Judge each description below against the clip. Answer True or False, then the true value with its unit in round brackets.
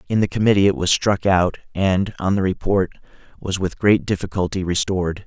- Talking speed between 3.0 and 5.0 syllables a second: False (5.4 syllables/s)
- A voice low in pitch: True (95 Hz)